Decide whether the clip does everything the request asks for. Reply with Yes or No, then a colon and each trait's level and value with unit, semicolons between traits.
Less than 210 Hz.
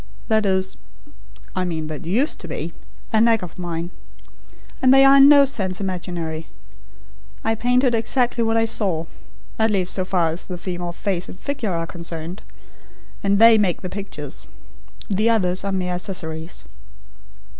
Yes: high, 190 Hz